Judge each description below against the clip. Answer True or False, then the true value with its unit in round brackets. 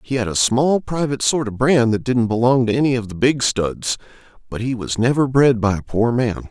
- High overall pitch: False (120 Hz)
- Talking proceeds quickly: True (240 wpm)